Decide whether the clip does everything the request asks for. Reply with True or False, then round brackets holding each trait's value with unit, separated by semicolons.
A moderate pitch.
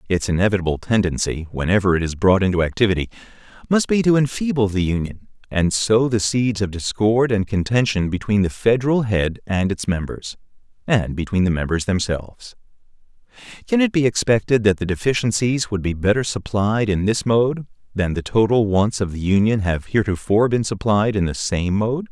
False (105 Hz)